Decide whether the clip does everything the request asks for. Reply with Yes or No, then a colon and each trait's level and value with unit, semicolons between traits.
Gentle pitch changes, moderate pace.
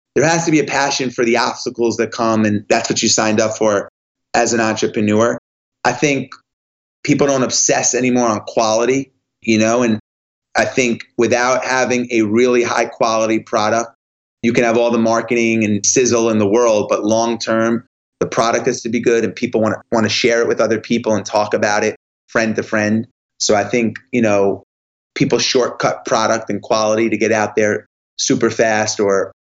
Yes: narrow, 1.9 semitones; average, 190 wpm